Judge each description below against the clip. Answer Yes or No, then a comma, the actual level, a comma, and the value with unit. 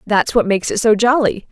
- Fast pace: Yes, fast, 235 wpm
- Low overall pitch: No, high, 220 Hz